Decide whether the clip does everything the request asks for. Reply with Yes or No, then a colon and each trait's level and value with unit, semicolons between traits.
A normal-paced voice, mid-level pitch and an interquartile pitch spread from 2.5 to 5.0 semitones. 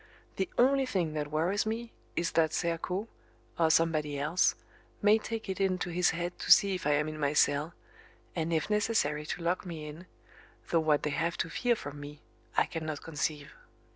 Yes: average, 190 wpm; medium, 165 Hz; average, 3.7 semitones